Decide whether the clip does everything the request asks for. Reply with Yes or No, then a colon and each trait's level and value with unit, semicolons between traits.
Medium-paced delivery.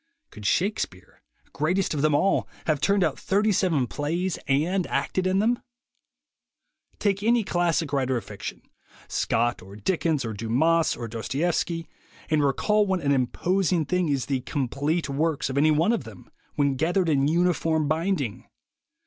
Yes: average, 155 wpm